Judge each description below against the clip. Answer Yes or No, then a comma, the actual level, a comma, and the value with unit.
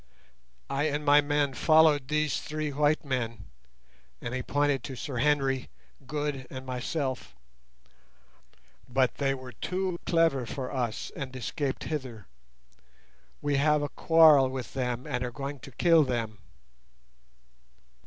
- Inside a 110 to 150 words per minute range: Yes, slow, 135 wpm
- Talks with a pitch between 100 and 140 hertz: Yes, low, 135 Hz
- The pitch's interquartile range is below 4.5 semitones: Yes, narrow, 2.6 semitones